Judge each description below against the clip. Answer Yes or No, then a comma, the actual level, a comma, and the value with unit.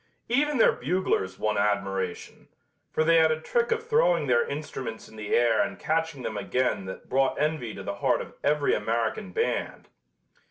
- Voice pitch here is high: No, low, 135 Hz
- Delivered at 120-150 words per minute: No, average, 175 wpm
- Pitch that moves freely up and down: Yes, wide, 7.0 semitones